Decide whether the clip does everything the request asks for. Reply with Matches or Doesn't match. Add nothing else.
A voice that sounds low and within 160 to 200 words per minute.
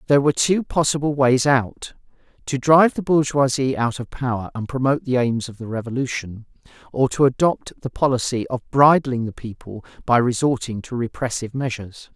Matches